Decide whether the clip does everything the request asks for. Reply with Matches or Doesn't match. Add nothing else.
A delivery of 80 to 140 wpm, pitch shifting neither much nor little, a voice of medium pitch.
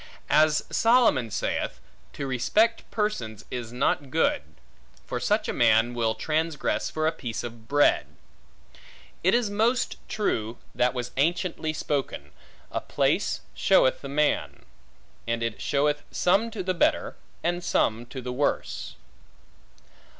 Doesn't match